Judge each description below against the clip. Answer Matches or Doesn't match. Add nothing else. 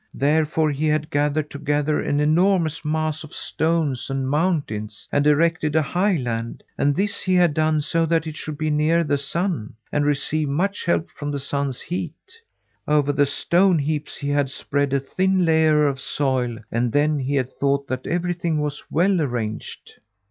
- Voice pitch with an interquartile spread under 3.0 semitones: Matches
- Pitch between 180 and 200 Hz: Doesn't match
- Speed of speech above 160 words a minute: Matches